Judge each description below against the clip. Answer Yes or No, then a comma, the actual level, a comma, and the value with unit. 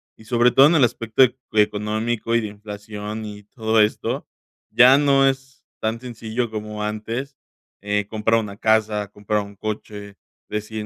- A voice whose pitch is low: Yes, low, 110 Hz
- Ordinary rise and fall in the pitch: No, narrow, 2.1 semitones